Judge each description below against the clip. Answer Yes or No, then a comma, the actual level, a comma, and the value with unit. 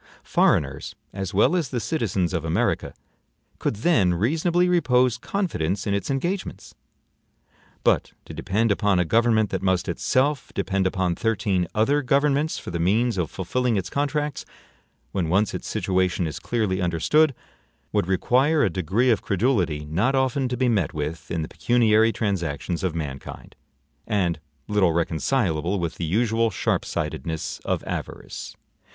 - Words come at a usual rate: Yes, average, 150 wpm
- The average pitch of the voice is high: No, low, 100 Hz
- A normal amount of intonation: No, wide, 6.2 semitones